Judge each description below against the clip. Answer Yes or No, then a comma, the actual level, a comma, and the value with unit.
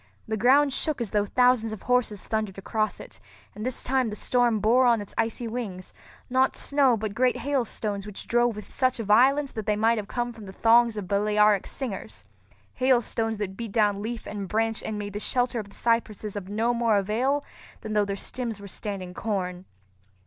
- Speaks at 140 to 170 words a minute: No, average, 195 wpm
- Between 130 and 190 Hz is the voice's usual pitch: No, high, 220 Hz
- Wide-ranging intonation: No, average, 2.8 semitones